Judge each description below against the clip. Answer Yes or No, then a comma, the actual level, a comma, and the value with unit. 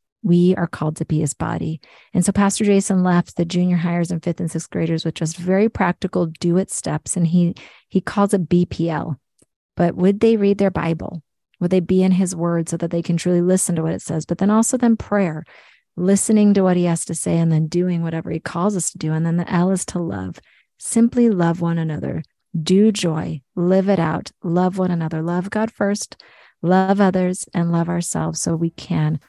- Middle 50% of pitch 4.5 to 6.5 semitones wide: No, narrow, 2.4 semitones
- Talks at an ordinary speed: No, fast, 215 wpm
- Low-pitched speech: No, medium, 175 Hz